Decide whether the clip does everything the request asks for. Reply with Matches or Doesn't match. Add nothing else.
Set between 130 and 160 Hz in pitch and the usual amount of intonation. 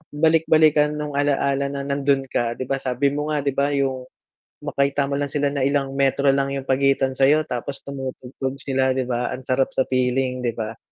Doesn't match